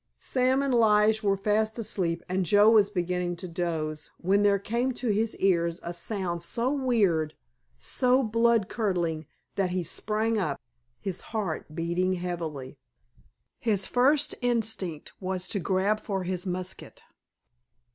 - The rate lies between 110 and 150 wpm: Yes, average, 140 wpm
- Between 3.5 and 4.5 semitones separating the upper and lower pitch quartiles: Yes, average, 4.1 semitones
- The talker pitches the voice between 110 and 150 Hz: No, high, 195 Hz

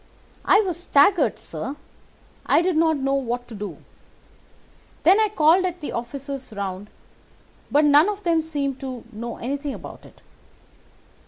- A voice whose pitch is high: Yes, very high, 285 Hz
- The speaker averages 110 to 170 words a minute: Yes, average, 150 wpm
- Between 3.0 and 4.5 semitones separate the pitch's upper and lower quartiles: No, average, 5.2 semitones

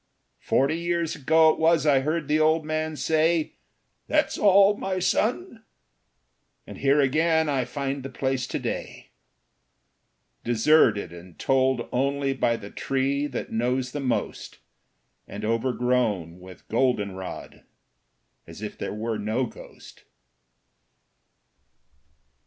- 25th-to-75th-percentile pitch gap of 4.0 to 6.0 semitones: Yes, average, 4.8 semitones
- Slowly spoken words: Yes, slow, 125 wpm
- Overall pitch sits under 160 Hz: Yes, low, 135 Hz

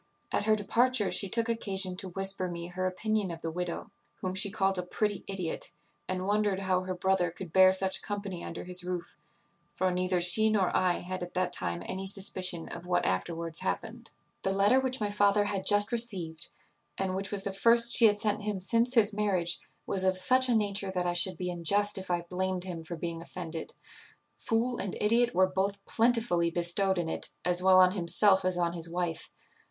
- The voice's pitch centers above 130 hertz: Yes, high, 190 Hz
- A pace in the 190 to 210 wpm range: Yes, fast, 205 wpm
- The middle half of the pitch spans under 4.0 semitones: Yes, narrow, 2.5 semitones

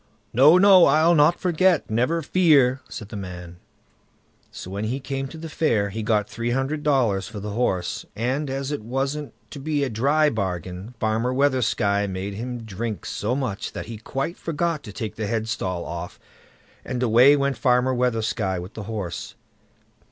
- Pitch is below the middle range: Yes, low, 120 Hz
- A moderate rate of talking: Yes, average, 175 wpm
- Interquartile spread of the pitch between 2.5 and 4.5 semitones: No, average, 5.2 semitones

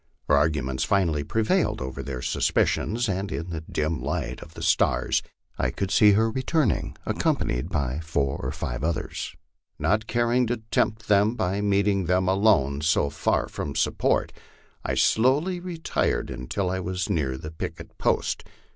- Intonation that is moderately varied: No, wide, 6.5 semitones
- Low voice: Yes, very low, 95 Hz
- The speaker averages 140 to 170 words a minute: Yes, average, 160 wpm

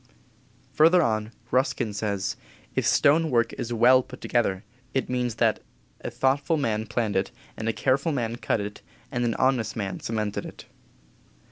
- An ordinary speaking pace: Yes, average, 160 wpm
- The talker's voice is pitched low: Yes, low, 120 Hz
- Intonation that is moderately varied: Yes, average, 3.2 semitones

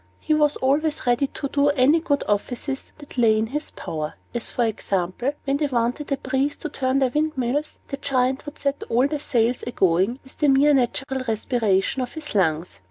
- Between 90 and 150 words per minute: No, fast, 205 wpm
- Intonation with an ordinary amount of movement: Yes, average, 3.5 semitones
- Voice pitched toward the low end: No, very high, 265 Hz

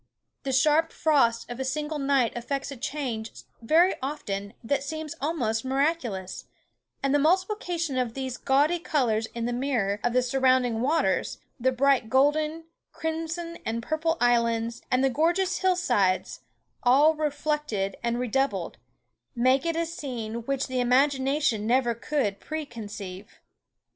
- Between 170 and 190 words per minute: No, average, 145 wpm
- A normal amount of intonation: Yes, average, 4.6 semitones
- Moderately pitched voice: No, very high, 265 Hz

